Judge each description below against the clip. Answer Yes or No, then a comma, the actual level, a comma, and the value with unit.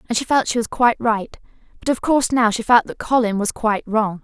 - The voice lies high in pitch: Yes, high, 230 Hz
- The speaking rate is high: Yes, fast, 255 wpm